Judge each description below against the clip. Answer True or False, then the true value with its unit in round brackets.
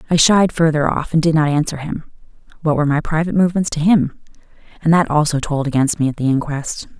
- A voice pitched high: False (155 Hz)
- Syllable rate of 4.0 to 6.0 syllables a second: False (6.3 syllables/s)